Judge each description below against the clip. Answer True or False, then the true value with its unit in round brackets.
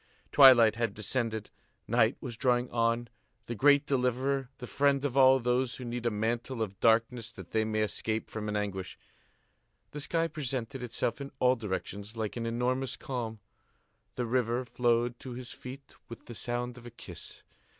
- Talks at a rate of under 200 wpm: True (170 wpm)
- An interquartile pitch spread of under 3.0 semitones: True (2.4 semitones)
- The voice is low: True (120 Hz)